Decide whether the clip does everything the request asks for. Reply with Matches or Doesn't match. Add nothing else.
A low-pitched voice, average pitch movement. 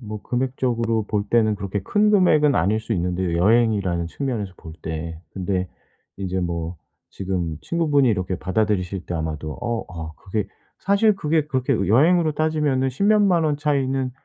Doesn't match